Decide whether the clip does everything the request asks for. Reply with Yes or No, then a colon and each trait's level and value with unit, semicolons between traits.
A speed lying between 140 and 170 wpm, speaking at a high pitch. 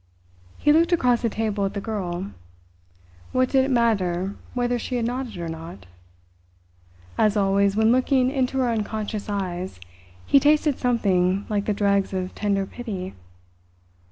Yes: average, 150 wpm; high, 215 Hz